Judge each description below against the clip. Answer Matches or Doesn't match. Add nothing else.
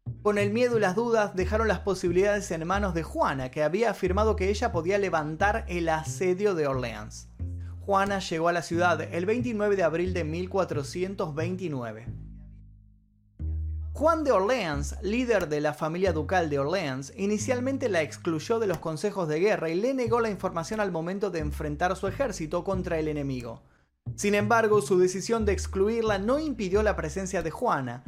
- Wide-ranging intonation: Matches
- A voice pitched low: Doesn't match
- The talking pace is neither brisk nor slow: Matches